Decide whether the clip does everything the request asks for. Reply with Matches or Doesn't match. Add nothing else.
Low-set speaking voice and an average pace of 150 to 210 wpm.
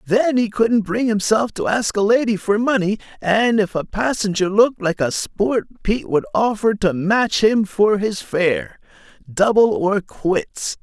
Doesn't match